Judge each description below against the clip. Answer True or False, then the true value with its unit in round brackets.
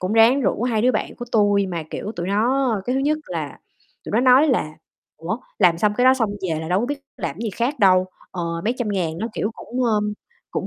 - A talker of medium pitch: False (220 Hz)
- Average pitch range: True (4.9 semitones)